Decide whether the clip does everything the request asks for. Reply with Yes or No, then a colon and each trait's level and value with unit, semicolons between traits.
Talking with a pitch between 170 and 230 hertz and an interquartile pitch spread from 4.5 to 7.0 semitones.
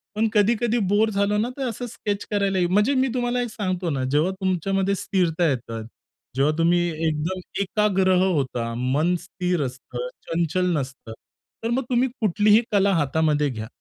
Yes: medium, 185 Hz; average, 5.2 semitones